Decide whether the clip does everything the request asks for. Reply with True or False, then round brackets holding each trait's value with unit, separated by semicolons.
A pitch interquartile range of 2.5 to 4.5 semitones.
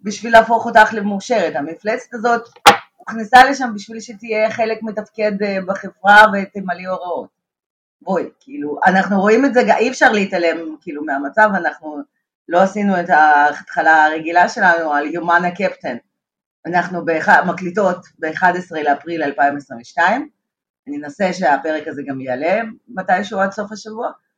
False (5.2 semitones)